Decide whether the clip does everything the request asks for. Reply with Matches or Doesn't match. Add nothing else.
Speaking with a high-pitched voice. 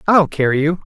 Doesn't match